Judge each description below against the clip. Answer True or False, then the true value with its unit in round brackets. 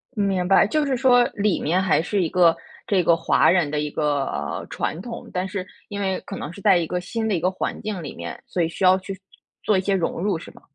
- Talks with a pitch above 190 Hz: False (185 Hz)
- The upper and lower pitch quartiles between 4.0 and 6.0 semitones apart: False (3.1 semitones)